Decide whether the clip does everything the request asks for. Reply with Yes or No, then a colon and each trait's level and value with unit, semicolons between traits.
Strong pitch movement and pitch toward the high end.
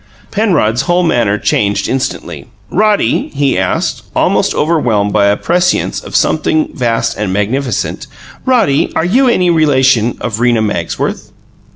No: wide, 8.5 semitones; low, 130 Hz